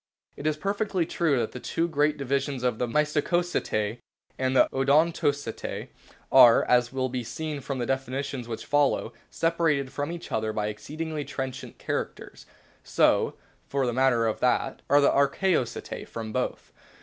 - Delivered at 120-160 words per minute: Yes, average, 155 wpm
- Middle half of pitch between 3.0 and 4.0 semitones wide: Yes, average, 3.6 semitones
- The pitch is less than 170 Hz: Yes, low, 135 Hz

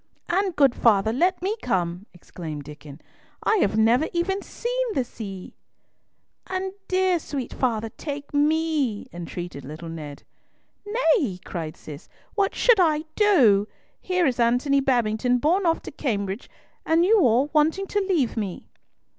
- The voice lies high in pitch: Yes, very high, 265 Hz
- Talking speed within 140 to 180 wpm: Yes, average, 145 wpm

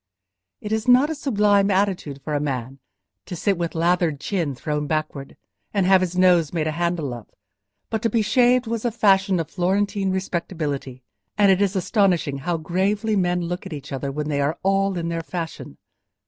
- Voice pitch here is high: No, medium, 180 Hz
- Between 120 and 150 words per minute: No, average, 190 wpm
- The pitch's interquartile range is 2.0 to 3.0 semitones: No, average, 4.6 semitones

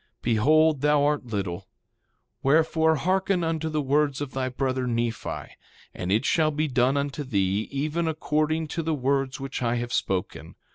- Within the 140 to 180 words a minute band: Yes, average, 160 wpm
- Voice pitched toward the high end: No, medium, 140 Hz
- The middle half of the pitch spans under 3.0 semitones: No, average, 4.0 semitones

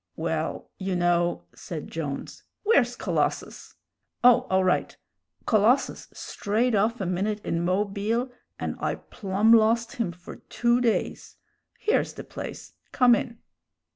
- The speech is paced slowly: Yes, slow, 130 wpm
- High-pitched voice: Yes, high, 215 Hz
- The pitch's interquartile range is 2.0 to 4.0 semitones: No, average, 4.5 semitones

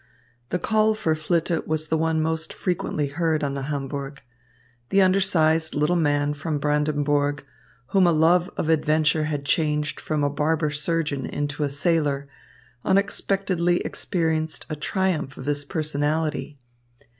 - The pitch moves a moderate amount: No, narrow, 2.2 semitones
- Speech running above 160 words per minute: No, average, 140 wpm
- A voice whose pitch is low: No, medium, 155 Hz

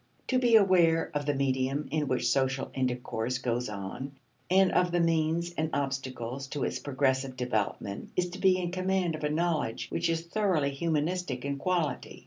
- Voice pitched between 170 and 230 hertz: No, medium, 145 Hz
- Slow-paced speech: No, average, 175 wpm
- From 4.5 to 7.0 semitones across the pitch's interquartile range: Yes, average, 4.9 semitones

